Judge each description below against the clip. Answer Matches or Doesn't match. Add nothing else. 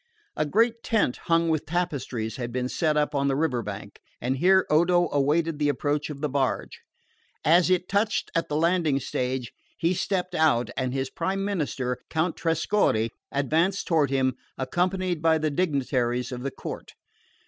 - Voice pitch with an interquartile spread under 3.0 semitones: Doesn't match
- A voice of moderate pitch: Matches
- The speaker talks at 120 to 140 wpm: Doesn't match